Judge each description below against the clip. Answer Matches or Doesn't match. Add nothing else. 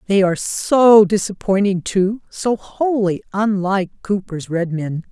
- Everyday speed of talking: Doesn't match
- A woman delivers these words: Matches